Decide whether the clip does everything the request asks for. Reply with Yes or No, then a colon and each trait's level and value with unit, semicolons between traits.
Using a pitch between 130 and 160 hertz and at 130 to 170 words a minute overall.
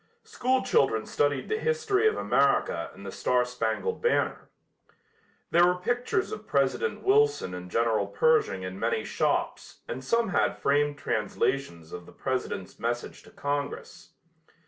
Yes: medium, 140 Hz; average, 145 wpm